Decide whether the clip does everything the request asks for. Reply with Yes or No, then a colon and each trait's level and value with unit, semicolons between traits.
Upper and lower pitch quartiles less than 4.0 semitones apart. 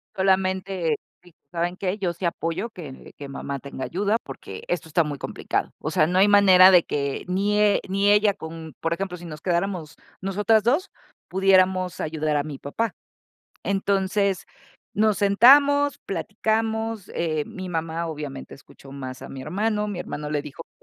No: average, 4.4 semitones